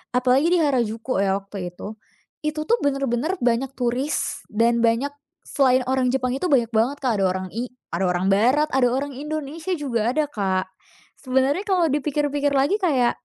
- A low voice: No, very high, 255 Hz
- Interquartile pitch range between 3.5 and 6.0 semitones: Yes, average, 4.1 semitones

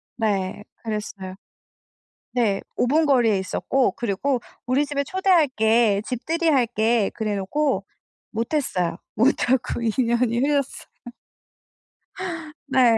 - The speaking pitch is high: Yes, high, 240 Hz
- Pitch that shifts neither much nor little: Yes, average, 4.5 semitones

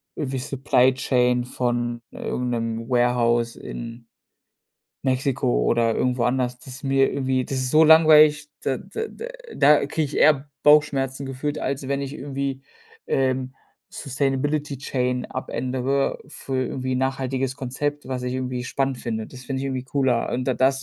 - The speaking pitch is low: Yes, low, 130 Hz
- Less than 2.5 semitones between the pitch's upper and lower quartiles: Yes, narrow, 1.8 semitones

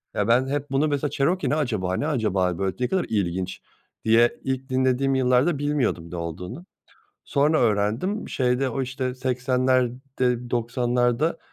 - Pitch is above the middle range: No, low, 125 Hz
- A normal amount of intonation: Yes, average, 3.3 semitones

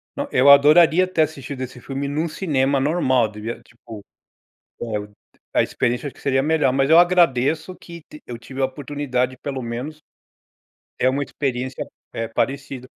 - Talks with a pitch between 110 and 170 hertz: Yes, low, 135 Hz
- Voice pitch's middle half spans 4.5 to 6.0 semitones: No, average, 3.1 semitones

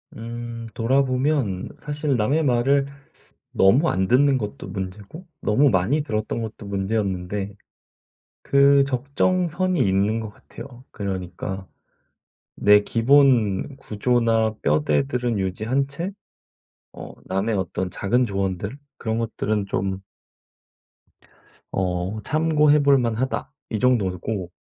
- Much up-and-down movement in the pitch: Yes, wide, 5.8 semitones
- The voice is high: No, low, 115 Hz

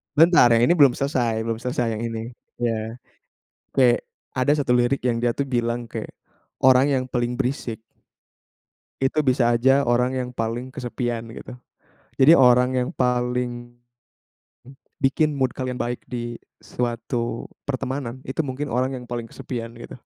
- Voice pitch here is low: Yes, low, 125 Hz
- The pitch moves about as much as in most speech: No, narrow, 1.7 semitones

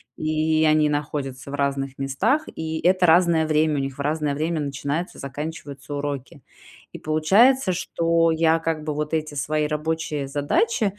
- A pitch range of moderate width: No, narrow, 2.2 semitones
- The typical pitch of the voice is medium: Yes, medium, 155 Hz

